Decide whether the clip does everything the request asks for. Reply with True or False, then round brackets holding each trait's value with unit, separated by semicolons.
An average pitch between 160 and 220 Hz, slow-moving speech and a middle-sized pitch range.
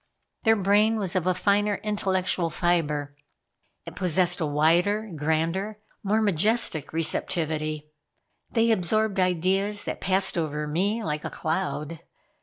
True (185 Hz; 125 wpm; 4.5 semitones)